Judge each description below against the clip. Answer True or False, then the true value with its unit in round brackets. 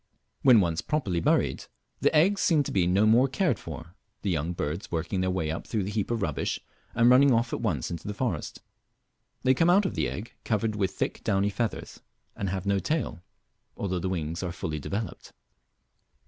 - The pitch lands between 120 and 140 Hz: False (100 Hz)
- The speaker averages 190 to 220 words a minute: True (200 wpm)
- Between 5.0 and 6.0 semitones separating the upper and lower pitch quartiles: True (5.5 semitones)